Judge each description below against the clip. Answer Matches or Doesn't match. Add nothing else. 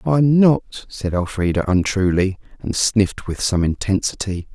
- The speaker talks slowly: Matches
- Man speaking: Matches